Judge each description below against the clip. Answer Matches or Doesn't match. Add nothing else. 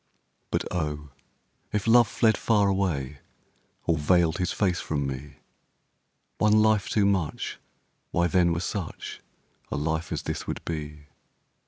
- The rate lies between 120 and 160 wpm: Matches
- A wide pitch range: Doesn't match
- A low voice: Matches